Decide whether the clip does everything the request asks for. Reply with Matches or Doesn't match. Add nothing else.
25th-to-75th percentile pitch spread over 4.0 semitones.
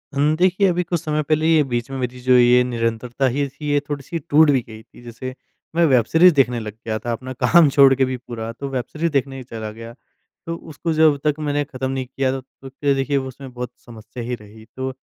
Doesn't match